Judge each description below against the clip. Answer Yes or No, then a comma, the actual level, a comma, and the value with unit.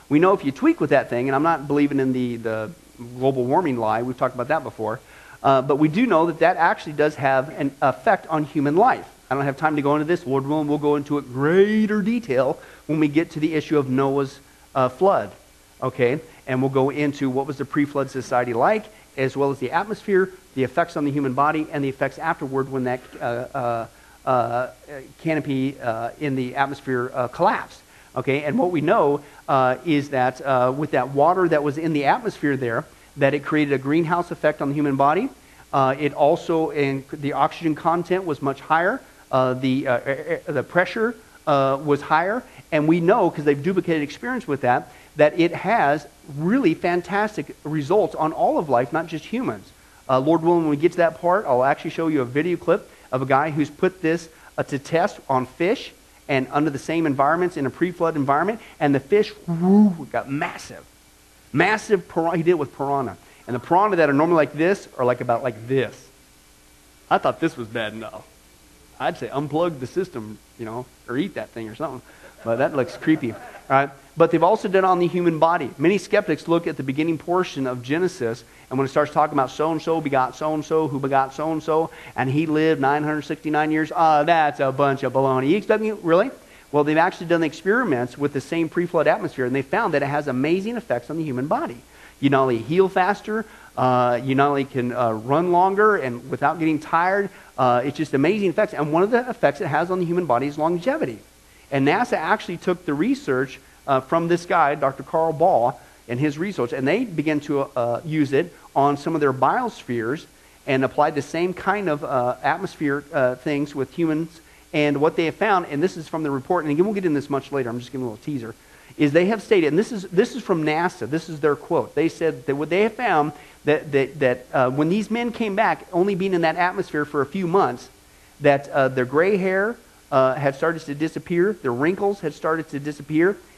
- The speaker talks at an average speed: No, fast, 220 wpm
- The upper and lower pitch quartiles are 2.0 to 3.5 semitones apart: No, average, 3.9 semitones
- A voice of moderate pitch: Yes, medium, 150 Hz